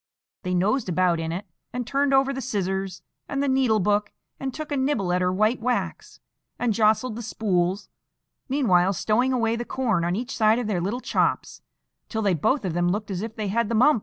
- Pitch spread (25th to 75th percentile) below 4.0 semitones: No, average, 5.1 semitones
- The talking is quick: Yes, fast, 215 wpm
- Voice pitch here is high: Yes, high, 215 Hz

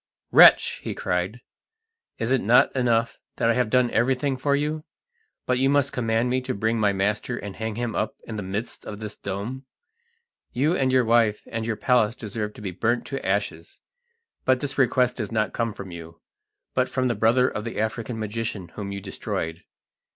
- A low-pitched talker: Yes, low, 115 Hz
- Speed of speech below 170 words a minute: No, average, 195 wpm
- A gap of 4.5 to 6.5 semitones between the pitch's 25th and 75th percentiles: No, average, 3.3 semitones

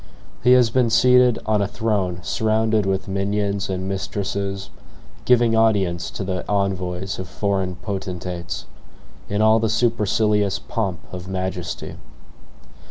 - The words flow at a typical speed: No, slow, 125 wpm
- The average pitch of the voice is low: Yes, low, 100 Hz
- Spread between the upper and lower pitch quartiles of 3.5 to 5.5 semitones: No, average, 2.8 semitones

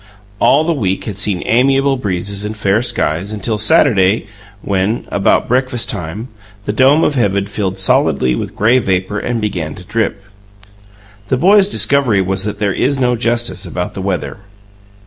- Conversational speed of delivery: Yes, average, 165 wpm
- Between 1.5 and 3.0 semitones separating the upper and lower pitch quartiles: No, average, 4.3 semitones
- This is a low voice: Yes, low, 105 Hz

